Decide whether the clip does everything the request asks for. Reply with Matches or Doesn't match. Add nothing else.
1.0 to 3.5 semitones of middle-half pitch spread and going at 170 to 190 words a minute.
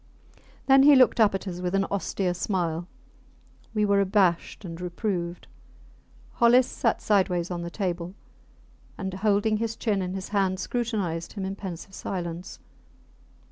Doesn't match